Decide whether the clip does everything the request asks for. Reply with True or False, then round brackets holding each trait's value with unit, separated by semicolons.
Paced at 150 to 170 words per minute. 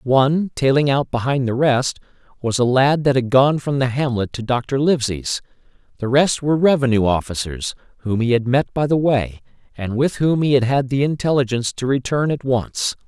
False (195 wpm)